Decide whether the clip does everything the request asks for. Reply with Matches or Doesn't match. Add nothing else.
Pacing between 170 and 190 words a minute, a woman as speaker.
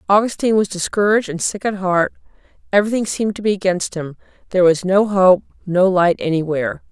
Matches